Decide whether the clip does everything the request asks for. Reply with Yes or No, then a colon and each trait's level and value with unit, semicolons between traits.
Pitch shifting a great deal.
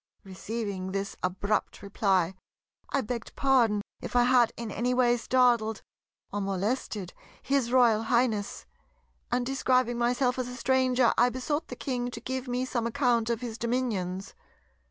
No: average, 3.1 semitones